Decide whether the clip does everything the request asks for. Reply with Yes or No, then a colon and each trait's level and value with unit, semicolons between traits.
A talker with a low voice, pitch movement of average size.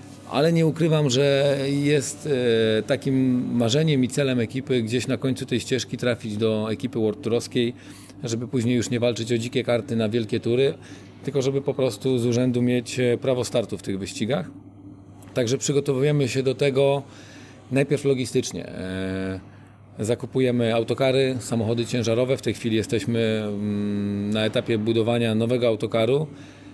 Yes: low, 120 Hz; average, 3.2 semitones